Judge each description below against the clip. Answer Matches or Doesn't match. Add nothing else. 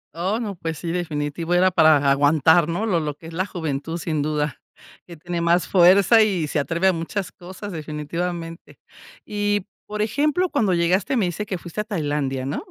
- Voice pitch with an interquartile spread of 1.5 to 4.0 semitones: Matches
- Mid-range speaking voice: Matches